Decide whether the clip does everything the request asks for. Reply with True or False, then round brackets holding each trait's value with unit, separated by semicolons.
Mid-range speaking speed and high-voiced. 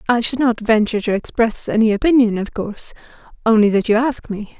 True (185 wpm; 225 Hz)